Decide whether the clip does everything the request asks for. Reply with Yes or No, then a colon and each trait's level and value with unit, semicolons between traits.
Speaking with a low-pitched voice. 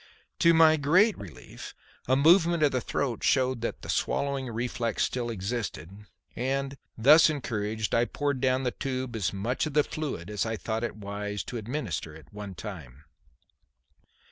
Yes: low, 120 Hz